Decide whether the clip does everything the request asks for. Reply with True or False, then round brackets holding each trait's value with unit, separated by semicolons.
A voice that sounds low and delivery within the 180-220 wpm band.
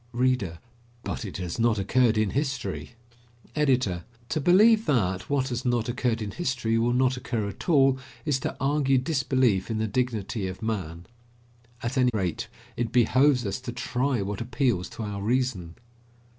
False (120 Hz; 165 wpm)